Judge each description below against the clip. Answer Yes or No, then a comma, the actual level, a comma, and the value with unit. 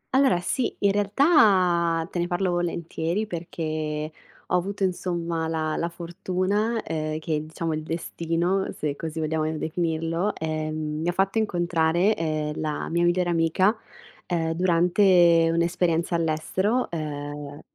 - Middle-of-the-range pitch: Yes, medium, 170 Hz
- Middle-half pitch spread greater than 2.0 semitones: Yes, narrow, 2.5 semitones